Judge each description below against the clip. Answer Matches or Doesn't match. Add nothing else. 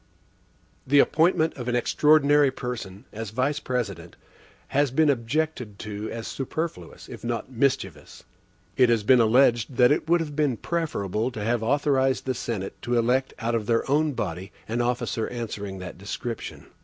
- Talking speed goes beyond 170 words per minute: Doesn't match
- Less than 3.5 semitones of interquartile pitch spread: Doesn't match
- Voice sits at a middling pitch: Doesn't match